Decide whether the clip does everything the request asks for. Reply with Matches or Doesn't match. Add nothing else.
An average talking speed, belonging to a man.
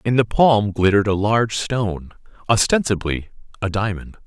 Doesn't match